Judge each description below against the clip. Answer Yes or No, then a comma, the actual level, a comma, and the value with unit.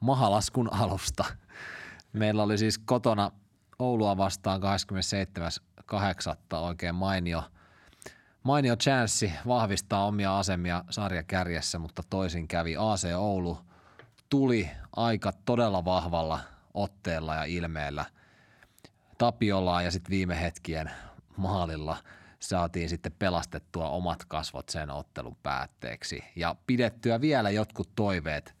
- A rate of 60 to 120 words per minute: Yes, average, 100 wpm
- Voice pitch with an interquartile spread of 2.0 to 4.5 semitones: Yes, average, 3.5 semitones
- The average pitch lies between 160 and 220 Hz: No, very low, 95 Hz